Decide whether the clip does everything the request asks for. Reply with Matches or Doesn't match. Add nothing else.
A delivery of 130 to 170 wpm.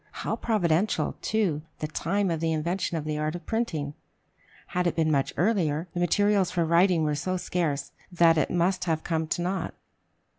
Doesn't match